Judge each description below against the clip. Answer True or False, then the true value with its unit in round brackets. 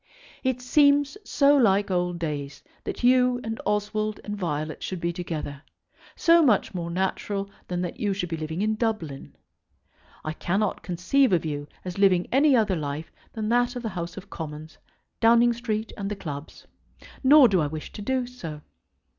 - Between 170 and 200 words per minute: True (175 wpm)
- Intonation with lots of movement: True (6.0 semitones)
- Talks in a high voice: True (195 Hz)